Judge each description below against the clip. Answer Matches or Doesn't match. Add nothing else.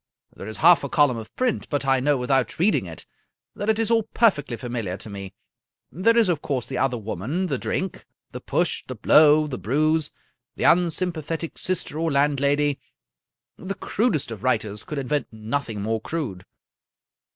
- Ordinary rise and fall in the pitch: Doesn't match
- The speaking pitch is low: Doesn't match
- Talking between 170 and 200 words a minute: Matches